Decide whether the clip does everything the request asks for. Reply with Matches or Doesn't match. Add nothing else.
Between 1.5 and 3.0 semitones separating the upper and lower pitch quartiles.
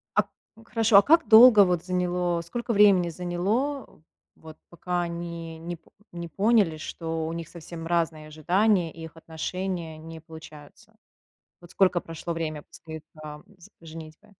Matches